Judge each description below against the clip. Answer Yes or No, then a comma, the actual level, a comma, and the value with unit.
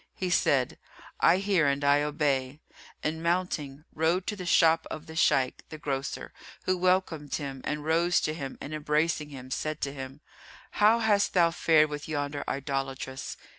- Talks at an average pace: Yes, average, 170 wpm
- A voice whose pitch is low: No, medium, 150 Hz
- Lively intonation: No, average, 3.2 semitones